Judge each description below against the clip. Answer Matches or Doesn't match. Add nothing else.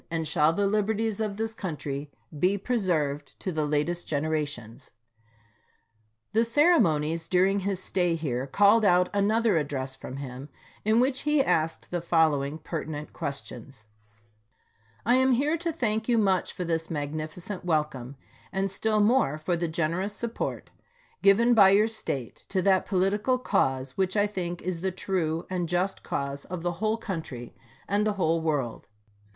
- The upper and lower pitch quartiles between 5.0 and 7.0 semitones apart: Matches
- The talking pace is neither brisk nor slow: Matches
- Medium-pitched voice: Matches